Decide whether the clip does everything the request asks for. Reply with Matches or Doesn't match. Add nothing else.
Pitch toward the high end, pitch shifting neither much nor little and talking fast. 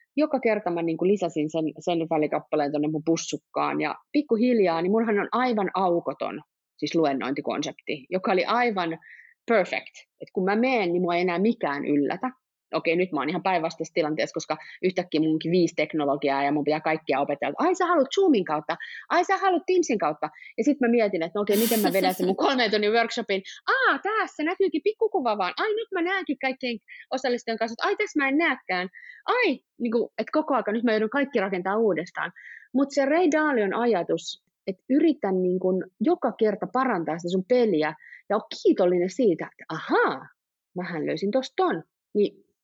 Doesn't match